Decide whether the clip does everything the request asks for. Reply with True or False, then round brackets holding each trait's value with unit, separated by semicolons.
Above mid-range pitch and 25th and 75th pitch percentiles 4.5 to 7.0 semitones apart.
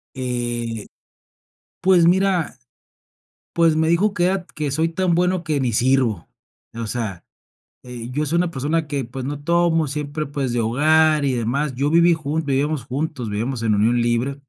False (145 Hz; 5.0 semitones)